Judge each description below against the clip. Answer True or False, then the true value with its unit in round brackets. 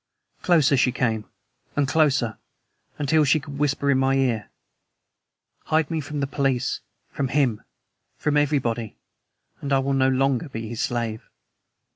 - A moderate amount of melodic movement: True (3.0 semitones)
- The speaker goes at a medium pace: True (145 wpm)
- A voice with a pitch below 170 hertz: True (135 Hz)